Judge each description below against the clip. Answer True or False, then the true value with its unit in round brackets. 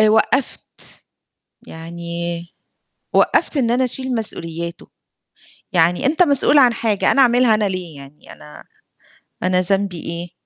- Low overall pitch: False (185 Hz)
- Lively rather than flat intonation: True (6.3 semitones)